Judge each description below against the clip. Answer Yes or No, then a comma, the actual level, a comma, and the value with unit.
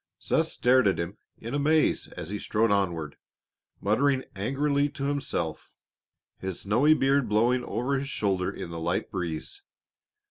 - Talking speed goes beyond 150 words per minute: No, average, 145 wpm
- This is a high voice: No, low, 115 Hz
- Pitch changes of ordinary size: No, wide, 6.7 semitones